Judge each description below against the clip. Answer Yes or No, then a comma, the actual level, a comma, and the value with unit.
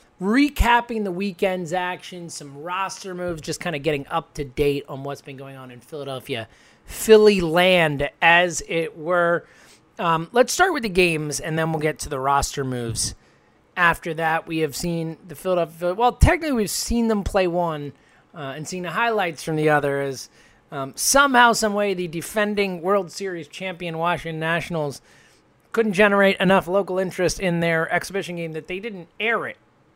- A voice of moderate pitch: Yes, medium, 170 Hz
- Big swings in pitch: No, average, 4.0 semitones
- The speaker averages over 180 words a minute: No, average, 175 wpm